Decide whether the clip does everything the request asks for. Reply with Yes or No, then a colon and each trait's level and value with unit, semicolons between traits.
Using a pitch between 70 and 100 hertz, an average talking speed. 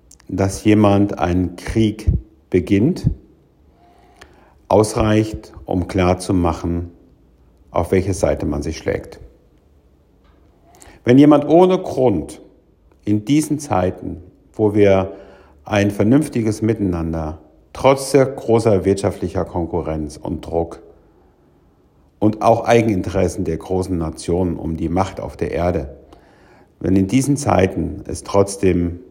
No: very low, 95 Hz; slow, 105 wpm